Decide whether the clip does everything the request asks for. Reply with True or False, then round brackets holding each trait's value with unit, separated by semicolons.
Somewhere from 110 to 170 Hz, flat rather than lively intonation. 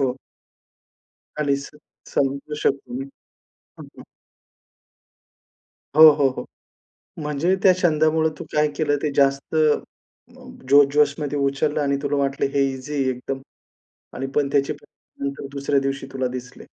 True (140 Hz; 1.6 semitones)